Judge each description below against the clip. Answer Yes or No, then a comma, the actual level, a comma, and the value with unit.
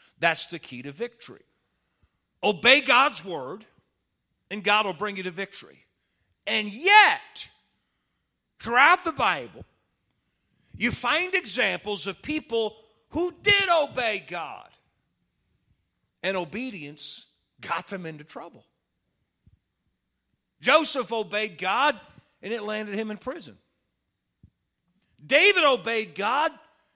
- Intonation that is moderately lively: No, wide, 7.7 semitones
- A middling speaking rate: No, slow, 105 wpm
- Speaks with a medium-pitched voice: No, high, 220 Hz